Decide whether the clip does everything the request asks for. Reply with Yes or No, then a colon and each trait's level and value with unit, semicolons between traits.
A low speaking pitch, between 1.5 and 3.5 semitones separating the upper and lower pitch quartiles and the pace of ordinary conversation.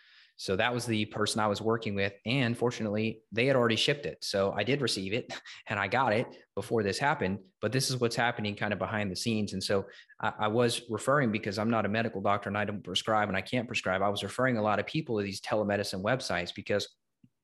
No: low, 105 Hz; narrow, 2.6 semitones; fast, 235 wpm